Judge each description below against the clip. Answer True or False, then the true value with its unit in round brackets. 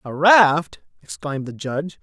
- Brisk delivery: False (150 wpm)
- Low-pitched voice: False (155 Hz)